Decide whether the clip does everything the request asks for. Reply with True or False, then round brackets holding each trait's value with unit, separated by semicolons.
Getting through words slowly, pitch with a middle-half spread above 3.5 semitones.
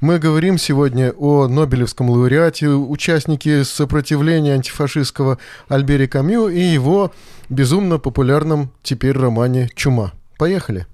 False (105 wpm; 3.1 semitones)